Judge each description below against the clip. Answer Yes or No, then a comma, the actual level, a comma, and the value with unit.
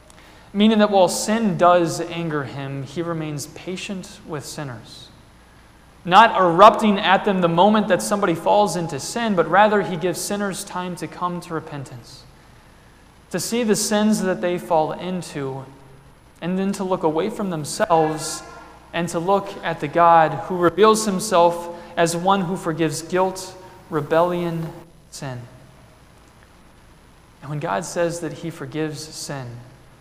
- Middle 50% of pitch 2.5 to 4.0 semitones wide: Yes, average, 3.5 semitones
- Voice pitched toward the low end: No, medium, 170 Hz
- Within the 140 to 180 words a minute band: Yes, average, 145 wpm